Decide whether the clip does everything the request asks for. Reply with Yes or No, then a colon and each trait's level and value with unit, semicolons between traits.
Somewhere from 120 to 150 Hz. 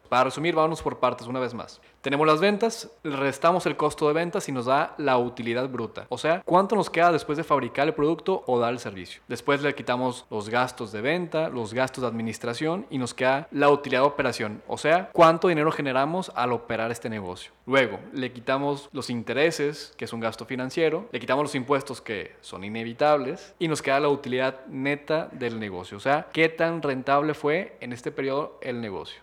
Yes: medium, 140 Hz